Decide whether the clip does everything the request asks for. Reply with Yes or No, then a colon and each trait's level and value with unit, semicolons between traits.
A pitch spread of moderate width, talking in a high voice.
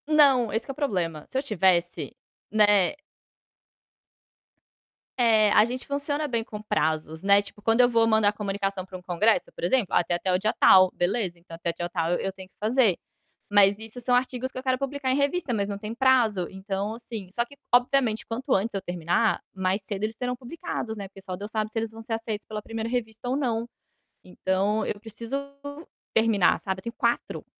Yes: average, 4.1 semitones; high, 215 Hz